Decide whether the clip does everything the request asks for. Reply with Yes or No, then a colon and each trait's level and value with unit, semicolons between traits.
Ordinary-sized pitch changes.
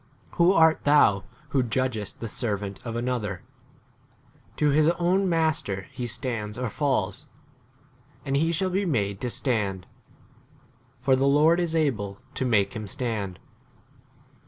No: wide, 6.6 semitones